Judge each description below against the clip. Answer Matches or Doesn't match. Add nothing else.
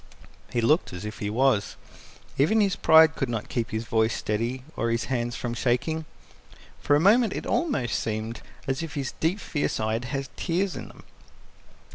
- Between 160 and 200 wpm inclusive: Matches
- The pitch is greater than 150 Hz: Doesn't match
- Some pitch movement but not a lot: Doesn't match